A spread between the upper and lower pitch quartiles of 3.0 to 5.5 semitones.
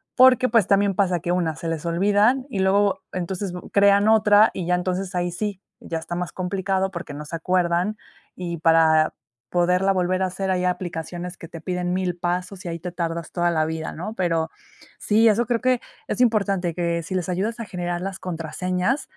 No: narrow, 2.5 semitones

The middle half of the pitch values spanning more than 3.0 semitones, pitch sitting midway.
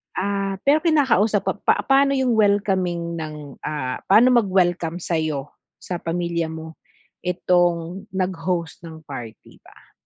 Yes: average, 3.8 semitones; medium, 175 Hz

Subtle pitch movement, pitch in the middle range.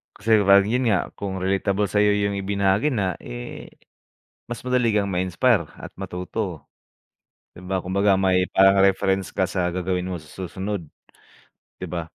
No: narrow, 1.7 semitones; very low, 95 Hz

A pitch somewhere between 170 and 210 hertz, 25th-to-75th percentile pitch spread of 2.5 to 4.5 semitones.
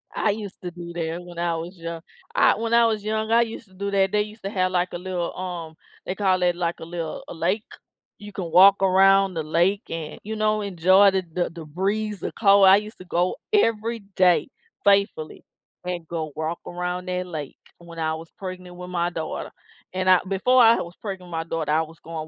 Yes: medium, 185 Hz; average, 2.9 semitones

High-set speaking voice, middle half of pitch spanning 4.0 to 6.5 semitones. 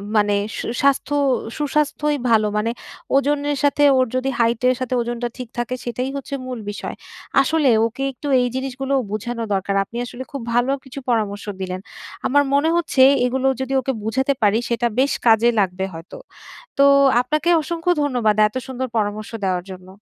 Yes: very high, 250 Hz; average, 4.3 semitones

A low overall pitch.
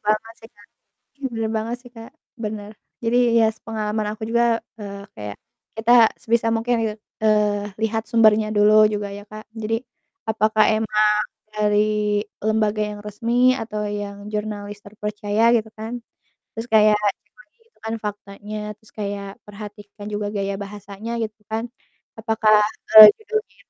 No: high, 215 Hz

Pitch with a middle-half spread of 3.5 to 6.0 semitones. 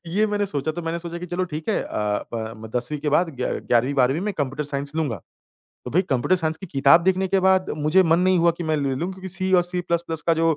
Yes: average, 4.3 semitones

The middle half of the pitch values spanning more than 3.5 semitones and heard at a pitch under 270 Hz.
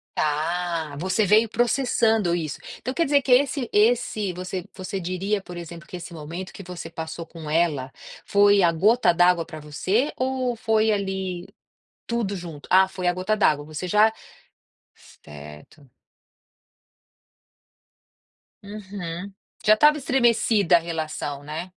Yes: average, 4.5 semitones; medium, 185 Hz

